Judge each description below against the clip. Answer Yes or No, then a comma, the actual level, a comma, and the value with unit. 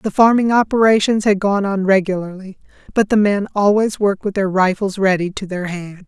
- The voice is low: No, high, 200 Hz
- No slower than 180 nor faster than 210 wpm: Yes, average, 190 wpm